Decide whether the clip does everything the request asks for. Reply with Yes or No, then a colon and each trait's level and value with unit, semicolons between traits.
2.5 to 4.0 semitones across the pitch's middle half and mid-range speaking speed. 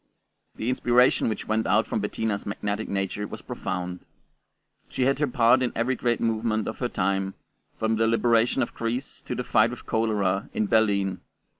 Yes: average, 2.9 semitones; average, 175 wpm